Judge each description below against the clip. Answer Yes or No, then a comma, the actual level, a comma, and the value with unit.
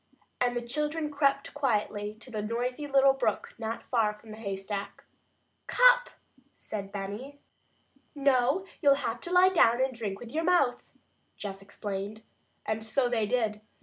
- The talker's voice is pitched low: No, high, 240 Hz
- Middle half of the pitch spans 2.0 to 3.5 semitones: No, average, 4.8 semitones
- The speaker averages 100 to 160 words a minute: Yes, average, 150 wpm